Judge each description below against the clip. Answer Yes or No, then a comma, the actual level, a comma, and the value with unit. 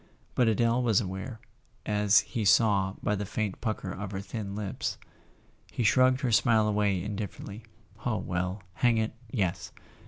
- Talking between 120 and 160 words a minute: Yes, average, 150 wpm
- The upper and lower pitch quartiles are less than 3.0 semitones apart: Yes, narrow, 2.6 semitones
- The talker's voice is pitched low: Yes, low, 105 Hz